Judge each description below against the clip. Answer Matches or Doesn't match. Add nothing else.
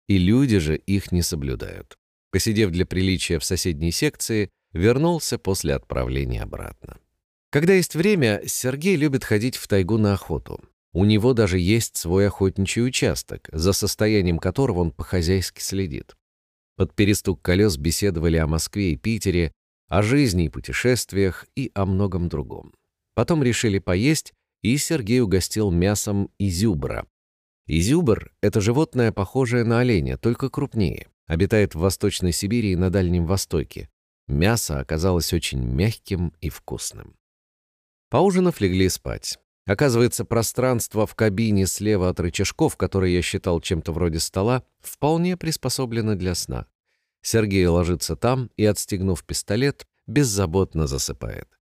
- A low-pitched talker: Matches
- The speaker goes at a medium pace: Matches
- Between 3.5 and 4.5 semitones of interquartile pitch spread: Doesn't match